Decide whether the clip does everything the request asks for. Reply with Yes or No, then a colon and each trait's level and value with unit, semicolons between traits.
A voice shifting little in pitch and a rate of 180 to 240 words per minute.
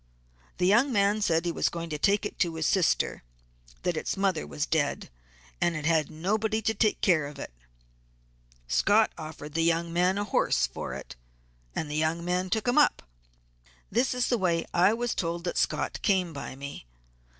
No: average, 4.2 semitones; average, 195 wpm